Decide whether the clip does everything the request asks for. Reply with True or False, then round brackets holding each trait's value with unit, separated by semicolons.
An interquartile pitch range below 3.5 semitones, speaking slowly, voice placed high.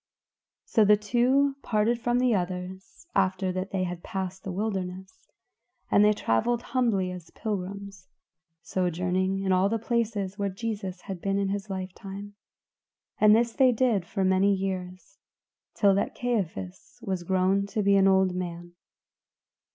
False (2.4 semitones; 155 wpm; 195 Hz)